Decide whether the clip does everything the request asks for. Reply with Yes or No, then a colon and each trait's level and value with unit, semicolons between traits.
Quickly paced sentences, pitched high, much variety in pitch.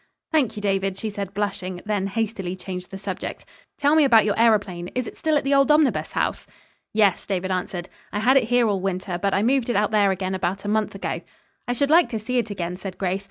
No: fast, 240 wpm; high, 205 Hz; average, 3.8 semitones